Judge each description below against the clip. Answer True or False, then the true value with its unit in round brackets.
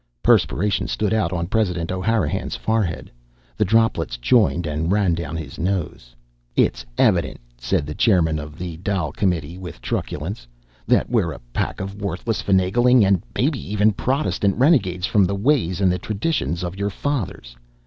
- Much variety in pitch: False (4.1 semitones)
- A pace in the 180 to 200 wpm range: False (160 wpm)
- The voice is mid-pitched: False (95 Hz)